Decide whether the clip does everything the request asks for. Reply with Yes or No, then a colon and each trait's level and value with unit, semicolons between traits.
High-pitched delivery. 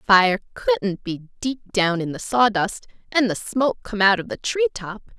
Yes: high, 215 Hz